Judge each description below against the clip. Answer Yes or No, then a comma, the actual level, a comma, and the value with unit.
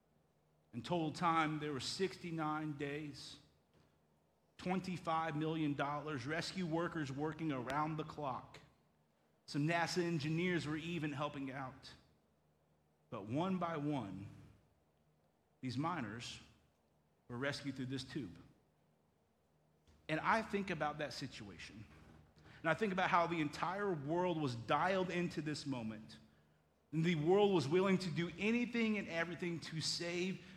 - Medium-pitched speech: Yes, medium, 150 Hz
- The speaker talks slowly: Yes, slow, 130 wpm